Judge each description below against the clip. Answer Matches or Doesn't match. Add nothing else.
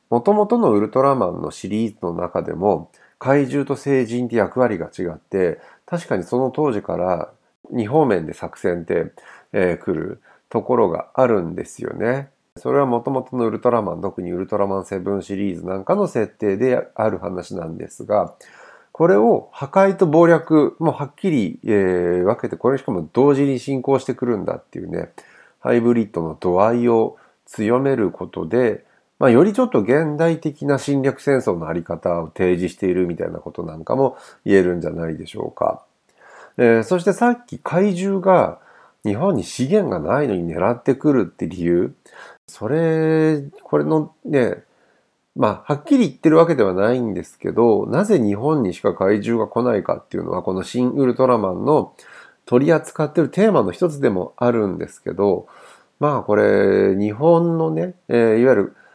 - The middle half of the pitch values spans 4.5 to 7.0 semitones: Doesn't match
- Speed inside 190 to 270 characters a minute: Doesn't match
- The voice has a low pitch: Matches